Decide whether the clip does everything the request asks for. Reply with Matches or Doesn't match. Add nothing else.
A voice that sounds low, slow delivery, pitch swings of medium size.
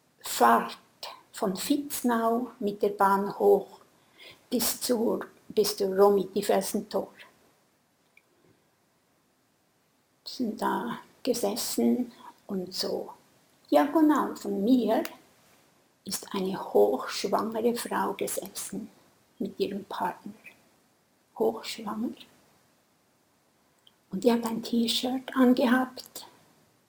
Doesn't match